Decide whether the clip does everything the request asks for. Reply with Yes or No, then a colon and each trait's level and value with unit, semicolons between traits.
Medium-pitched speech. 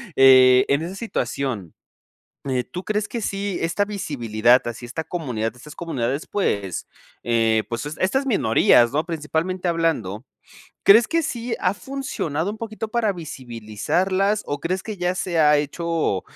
Yes: medium, 160 Hz